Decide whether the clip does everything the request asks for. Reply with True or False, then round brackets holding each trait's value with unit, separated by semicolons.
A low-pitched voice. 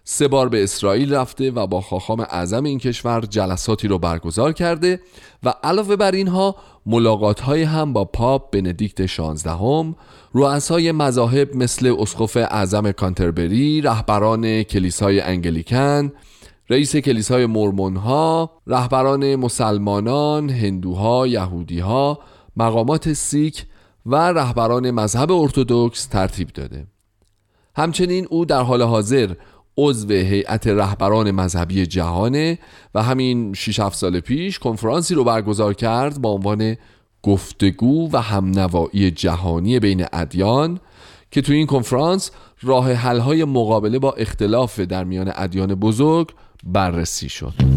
True (115 Hz)